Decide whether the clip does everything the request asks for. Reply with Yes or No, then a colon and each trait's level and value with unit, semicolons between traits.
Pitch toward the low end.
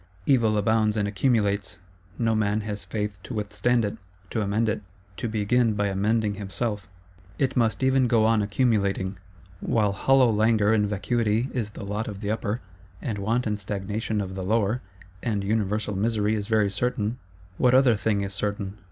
Yes: low, 105 Hz